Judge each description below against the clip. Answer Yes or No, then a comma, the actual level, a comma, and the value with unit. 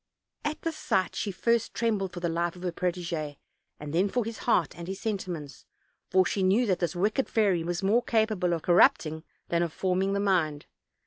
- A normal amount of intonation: Yes, average, 3.4 semitones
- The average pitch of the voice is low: No, medium, 185 Hz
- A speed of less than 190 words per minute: No, fast, 205 wpm